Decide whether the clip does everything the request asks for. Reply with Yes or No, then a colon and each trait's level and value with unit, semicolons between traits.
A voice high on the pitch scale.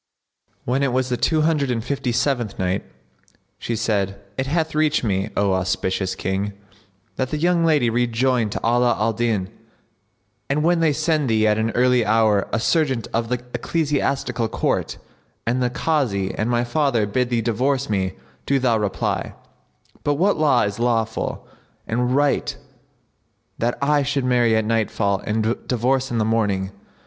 No: low, 120 Hz